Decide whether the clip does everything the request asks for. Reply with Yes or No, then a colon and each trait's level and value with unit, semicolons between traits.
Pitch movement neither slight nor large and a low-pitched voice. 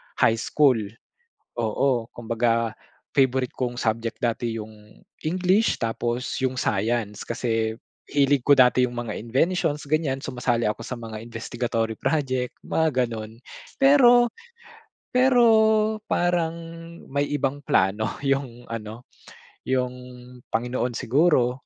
Yes: average, 3.7 semitones; low, 125 Hz